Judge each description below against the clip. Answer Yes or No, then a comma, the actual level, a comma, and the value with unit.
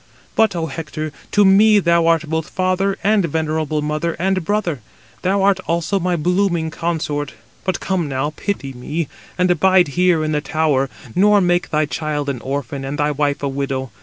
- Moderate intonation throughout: Yes, average, 3.9 semitones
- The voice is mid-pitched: Yes, medium, 160 Hz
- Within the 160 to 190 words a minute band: Yes, average, 180 wpm